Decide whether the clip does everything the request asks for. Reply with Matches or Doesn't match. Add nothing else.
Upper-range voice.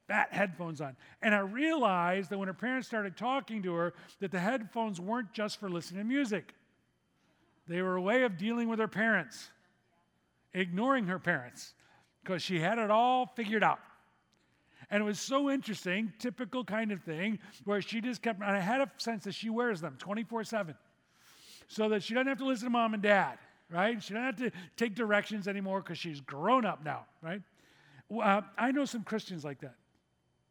Matches